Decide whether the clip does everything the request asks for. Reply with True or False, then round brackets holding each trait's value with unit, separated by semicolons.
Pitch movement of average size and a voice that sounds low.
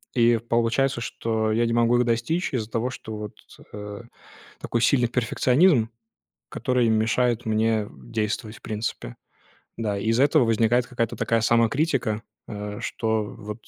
False (1.9 semitones; 115 Hz)